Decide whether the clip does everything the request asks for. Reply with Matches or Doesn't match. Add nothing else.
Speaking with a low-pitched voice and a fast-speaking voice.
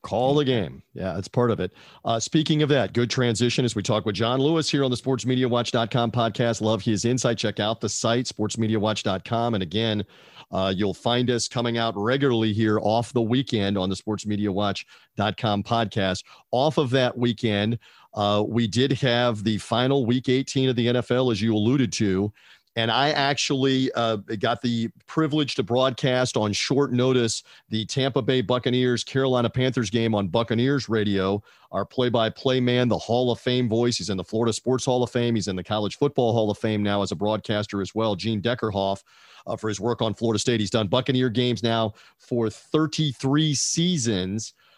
Doesn't match